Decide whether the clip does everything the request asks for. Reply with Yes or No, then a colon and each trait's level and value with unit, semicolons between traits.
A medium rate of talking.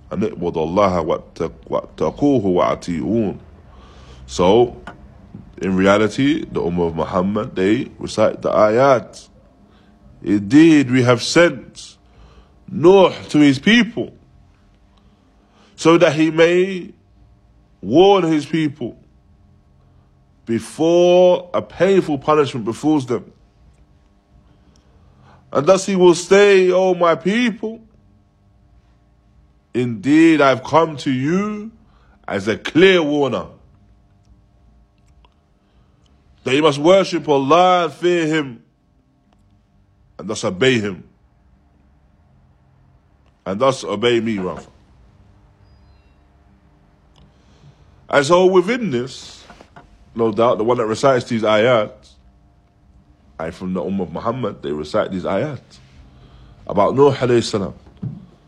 No: slow, 95 wpm